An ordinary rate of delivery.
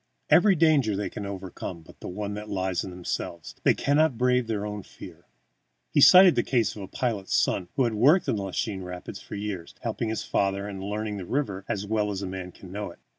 No: fast, 225 wpm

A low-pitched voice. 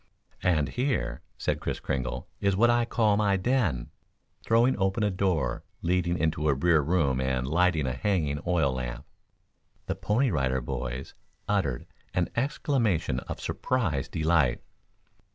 Yes: very low, 85 Hz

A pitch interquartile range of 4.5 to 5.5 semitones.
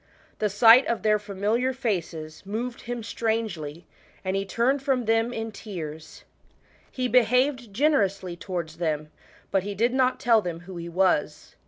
Yes: average, 5.2 semitones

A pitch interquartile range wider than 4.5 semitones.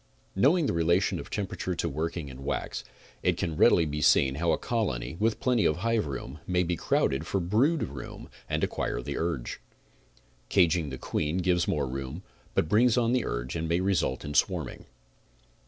Yes: wide, 5.5 semitones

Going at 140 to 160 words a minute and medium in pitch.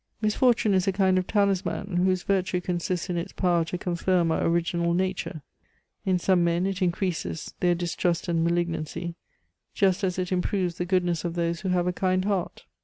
No: average, 180 wpm; medium, 180 Hz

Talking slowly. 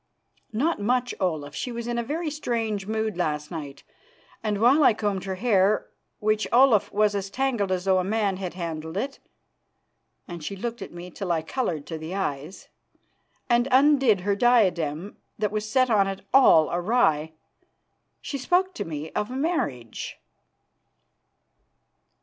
No: average, 155 wpm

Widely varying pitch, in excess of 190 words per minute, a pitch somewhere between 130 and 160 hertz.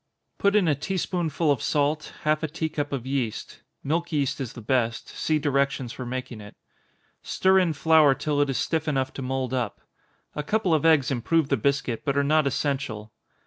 No: average, 3.1 semitones; average, 200 wpm; medium, 140 Hz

